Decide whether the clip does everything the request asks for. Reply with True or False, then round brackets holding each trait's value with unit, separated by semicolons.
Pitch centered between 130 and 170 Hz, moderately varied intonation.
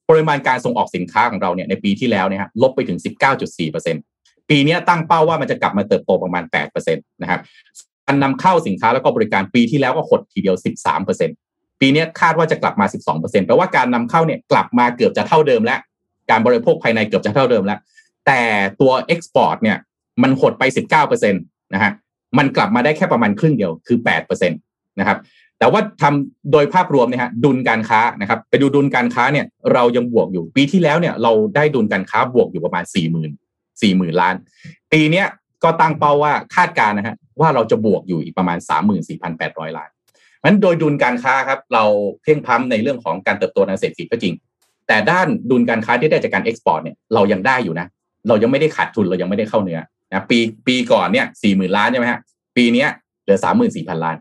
False (140 Hz; 6.3 semitones)